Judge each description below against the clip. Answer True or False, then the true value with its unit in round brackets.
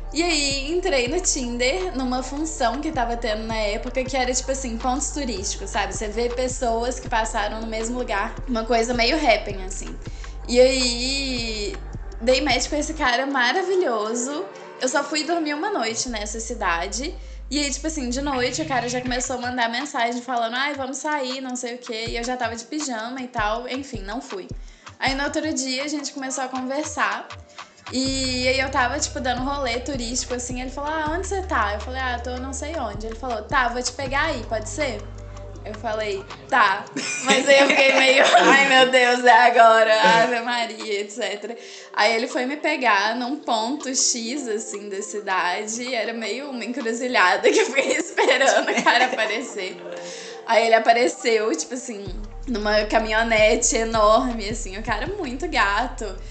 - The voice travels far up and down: False (3.4 semitones)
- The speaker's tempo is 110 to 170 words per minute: False (185 wpm)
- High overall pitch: True (250 Hz)